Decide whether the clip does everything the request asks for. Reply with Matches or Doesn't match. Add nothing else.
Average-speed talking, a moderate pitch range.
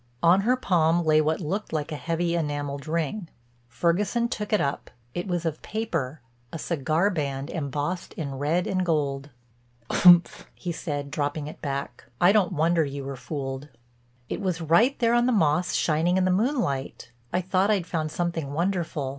Matches